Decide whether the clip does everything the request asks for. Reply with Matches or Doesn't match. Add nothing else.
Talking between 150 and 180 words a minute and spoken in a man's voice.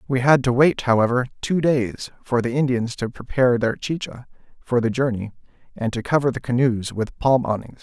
Doesn't match